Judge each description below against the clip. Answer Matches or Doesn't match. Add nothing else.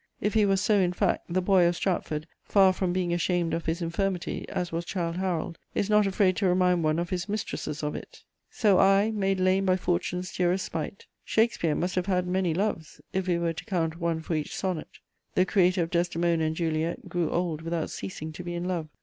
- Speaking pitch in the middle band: Matches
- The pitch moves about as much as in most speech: Doesn't match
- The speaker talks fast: Matches